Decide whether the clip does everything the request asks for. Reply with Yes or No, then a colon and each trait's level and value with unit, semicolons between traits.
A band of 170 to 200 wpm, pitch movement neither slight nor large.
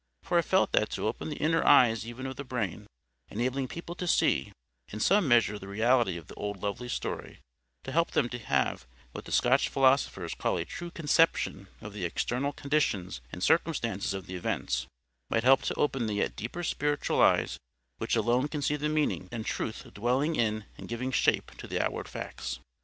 No: average, 195 wpm; wide, 5.7 semitones